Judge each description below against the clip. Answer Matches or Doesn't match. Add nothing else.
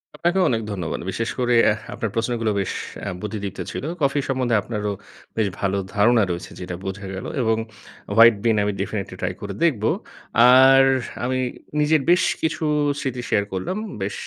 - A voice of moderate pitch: Doesn't match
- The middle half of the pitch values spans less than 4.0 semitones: Doesn't match